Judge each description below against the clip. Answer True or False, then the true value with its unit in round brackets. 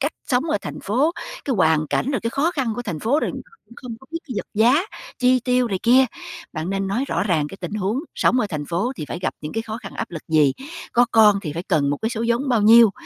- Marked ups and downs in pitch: True (6.1 semitones)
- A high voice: True (225 Hz)